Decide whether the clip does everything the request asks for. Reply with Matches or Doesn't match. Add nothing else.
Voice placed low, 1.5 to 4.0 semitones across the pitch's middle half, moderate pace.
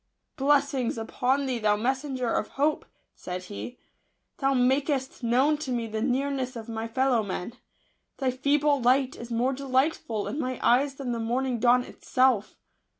Doesn't match